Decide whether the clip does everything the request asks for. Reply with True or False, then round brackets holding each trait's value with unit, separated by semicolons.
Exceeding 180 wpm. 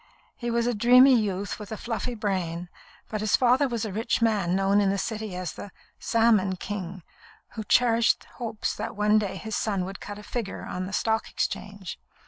True (195 wpm)